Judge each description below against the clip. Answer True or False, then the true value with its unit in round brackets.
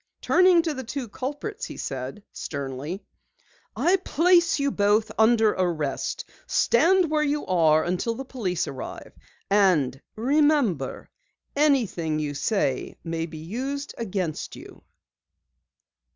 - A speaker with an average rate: False (120 wpm)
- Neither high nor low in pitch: False (215 Hz)